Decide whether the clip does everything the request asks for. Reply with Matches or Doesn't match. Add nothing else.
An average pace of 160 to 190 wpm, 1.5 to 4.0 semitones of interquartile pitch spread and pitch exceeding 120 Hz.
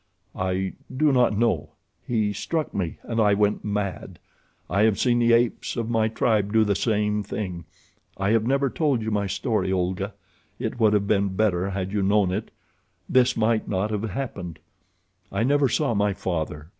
Doesn't match